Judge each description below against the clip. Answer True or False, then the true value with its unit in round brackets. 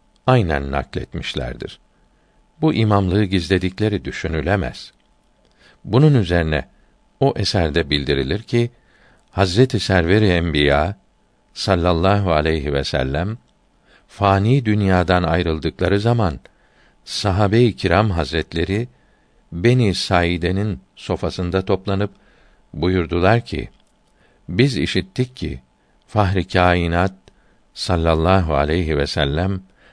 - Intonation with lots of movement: False (3.7 semitones)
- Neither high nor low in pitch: False (95 Hz)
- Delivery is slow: True (80 wpm)